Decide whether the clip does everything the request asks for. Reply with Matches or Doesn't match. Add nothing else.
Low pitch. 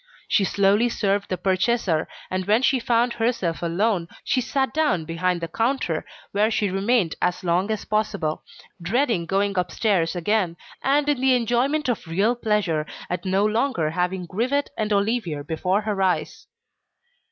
Doesn't match